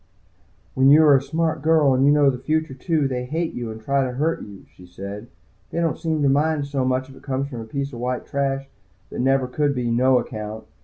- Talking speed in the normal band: No, fast, 250 wpm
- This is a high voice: No, low, 135 Hz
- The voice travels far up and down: No, average, 2.9 semitones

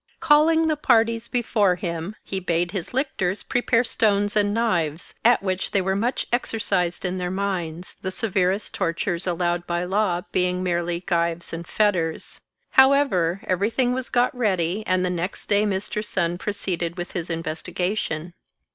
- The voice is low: No, high, 190 Hz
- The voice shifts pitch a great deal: No, average, 3.8 semitones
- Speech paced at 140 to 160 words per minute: Yes, average, 155 wpm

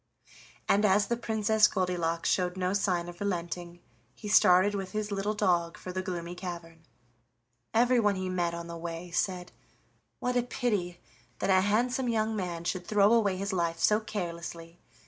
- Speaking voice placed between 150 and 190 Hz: Yes, medium, 185 Hz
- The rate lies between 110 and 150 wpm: No, average, 165 wpm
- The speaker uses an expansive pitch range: No, average, 3.3 semitones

